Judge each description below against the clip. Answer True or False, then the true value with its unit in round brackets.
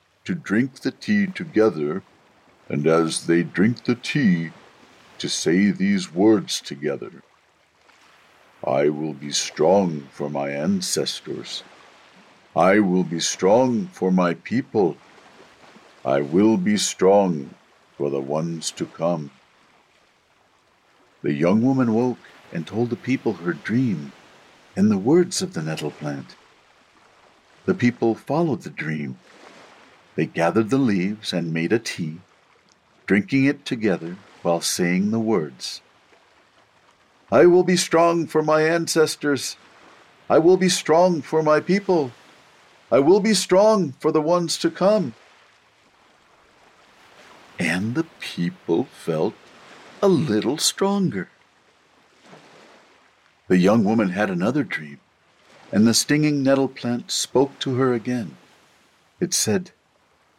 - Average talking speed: False (120 wpm)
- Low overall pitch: True (120 Hz)